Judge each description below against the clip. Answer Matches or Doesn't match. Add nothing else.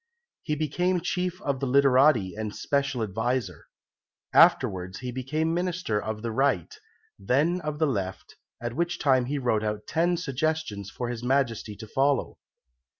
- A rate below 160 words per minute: Matches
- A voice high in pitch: Doesn't match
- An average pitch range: Doesn't match